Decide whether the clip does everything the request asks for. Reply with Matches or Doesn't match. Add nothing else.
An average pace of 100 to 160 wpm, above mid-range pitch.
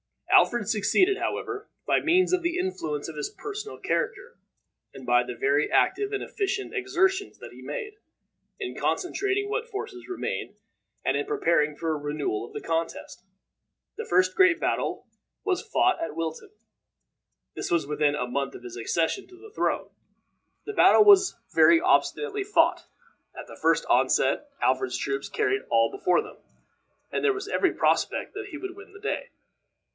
Doesn't match